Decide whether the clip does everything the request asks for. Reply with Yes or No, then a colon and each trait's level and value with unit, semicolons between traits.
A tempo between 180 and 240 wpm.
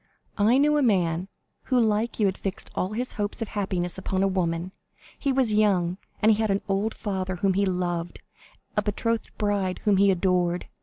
Yes: average, 190 wpm